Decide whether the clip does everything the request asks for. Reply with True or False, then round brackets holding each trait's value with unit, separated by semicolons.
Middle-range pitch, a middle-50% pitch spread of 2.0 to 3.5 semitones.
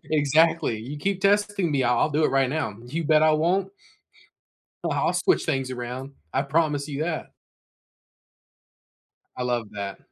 False (150 Hz; 4.2 semitones)